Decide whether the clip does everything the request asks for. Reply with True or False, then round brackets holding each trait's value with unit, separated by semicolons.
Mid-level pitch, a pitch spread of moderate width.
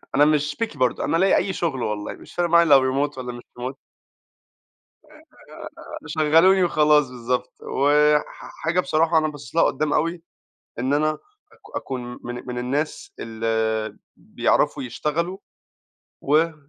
True (150 Hz; 4.2 semitones)